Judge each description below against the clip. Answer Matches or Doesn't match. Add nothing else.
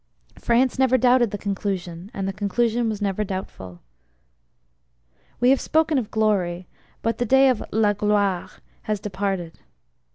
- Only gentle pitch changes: Doesn't match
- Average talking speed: Matches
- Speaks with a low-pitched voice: Doesn't match